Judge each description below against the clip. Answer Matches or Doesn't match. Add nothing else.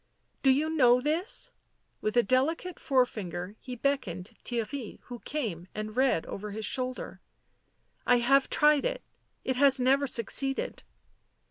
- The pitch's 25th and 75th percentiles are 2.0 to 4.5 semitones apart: Matches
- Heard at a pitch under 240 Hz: Doesn't match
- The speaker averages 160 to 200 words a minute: Doesn't match